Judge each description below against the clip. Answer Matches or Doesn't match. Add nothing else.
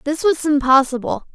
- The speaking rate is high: Doesn't match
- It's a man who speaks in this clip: Doesn't match